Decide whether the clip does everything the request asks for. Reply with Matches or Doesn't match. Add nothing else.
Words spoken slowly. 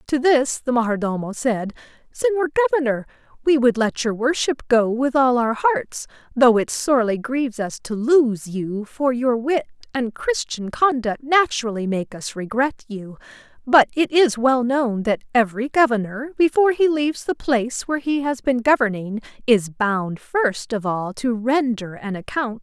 Doesn't match